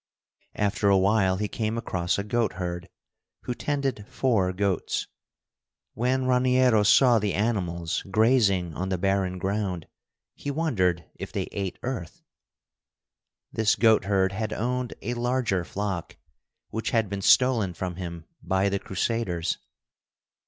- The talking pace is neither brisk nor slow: No, slow, 130 wpm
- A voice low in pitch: Yes, low, 100 Hz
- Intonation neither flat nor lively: Yes, average, 4.0 semitones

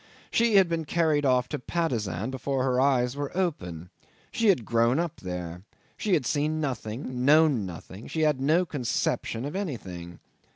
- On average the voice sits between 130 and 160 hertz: Yes, low, 135 Hz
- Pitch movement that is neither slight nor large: No, wide, 5.8 semitones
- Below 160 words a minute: No, average, 175 wpm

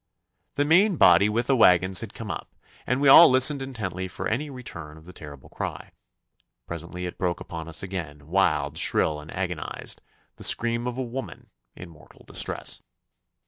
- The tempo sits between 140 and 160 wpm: No, average, 175 wpm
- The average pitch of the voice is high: No, very low, 95 Hz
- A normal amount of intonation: No, wide, 7.0 semitones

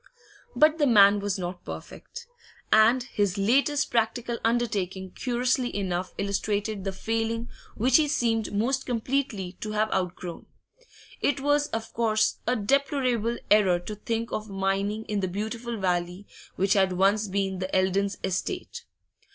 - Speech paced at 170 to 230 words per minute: No, average, 145 wpm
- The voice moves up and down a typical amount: Yes, average, 3.8 semitones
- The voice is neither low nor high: No, high, 215 Hz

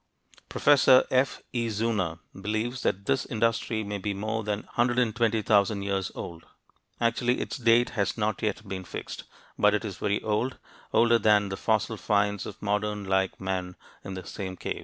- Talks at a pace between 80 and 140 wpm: No, average, 165 wpm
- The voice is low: Yes, low, 105 Hz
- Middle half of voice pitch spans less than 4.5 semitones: Yes, average, 2.7 semitones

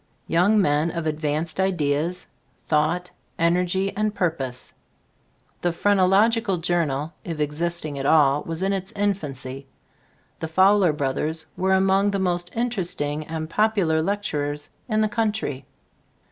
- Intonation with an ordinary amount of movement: Yes, average, 4.3 semitones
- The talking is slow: Yes, slow, 130 wpm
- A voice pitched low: No, medium, 170 Hz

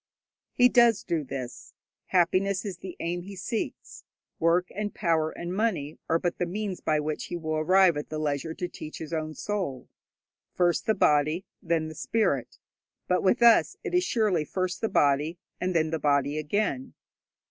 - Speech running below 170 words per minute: No, average, 180 wpm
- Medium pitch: Yes, medium, 170 Hz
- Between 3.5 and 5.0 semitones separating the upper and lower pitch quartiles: Yes, average, 4.0 semitones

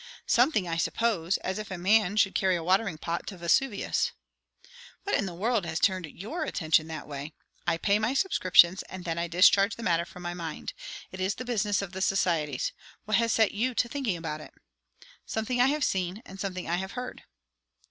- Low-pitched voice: No, high, 190 Hz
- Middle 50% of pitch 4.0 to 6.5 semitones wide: Yes, average, 4.4 semitones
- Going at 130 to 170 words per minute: No, fast, 205 wpm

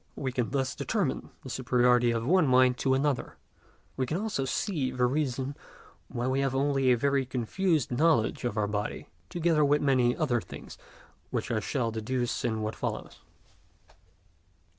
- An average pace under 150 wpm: No, average, 160 wpm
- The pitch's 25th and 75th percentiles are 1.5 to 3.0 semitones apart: Yes, average, 2.7 semitones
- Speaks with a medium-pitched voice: No, low, 130 Hz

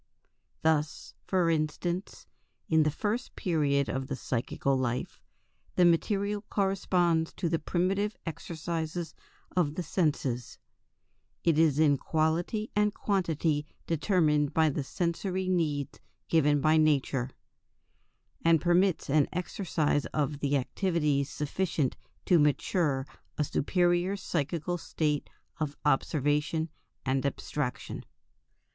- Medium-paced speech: No, slow, 110 wpm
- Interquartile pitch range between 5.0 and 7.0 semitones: No, average, 3.3 semitones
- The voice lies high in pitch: No, medium, 160 Hz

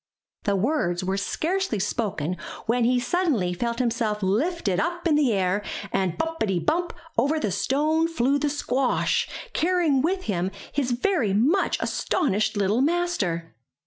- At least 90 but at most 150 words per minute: Yes, average, 145 wpm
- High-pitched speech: Yes, high, 245 Hz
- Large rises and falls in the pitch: Yes, wide, 8.1 semitones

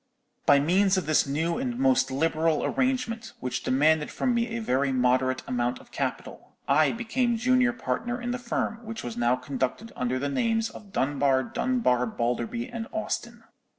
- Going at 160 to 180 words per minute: Yes, average, 170 wpm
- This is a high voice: No, medium, 170 Hz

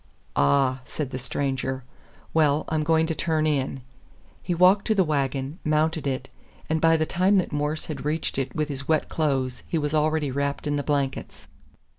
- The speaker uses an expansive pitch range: No, average, 2.8 semitones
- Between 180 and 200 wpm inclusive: Yes, average, 185 wpm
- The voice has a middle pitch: Yes, medium, 150 Hz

